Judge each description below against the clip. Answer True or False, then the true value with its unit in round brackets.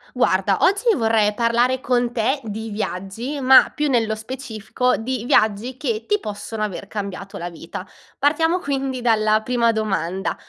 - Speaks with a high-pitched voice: True (225 Hz)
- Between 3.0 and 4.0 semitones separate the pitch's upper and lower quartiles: True (3.7 semitones)